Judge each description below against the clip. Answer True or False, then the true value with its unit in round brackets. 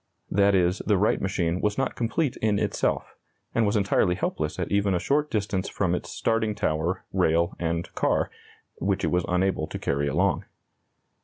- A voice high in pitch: False (95 Hz)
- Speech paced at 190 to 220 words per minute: False (175 wpm)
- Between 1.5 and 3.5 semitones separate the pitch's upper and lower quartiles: True (3.1 semitones)